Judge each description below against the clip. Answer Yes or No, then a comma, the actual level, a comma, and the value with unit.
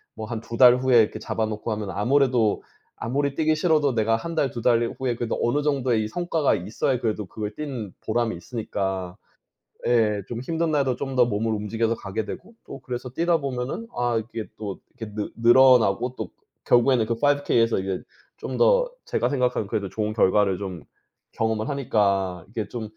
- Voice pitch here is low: Yes, low, 115 Hz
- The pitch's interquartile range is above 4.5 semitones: No, average, 3.9 semitones